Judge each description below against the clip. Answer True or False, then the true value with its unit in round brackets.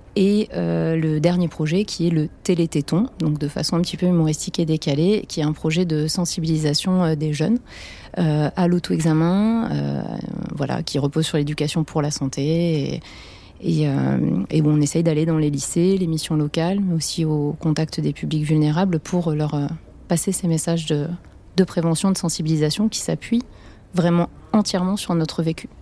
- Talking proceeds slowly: False (180 wpm)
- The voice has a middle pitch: True (165 Hz)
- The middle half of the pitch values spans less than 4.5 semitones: True (2.7 semitones)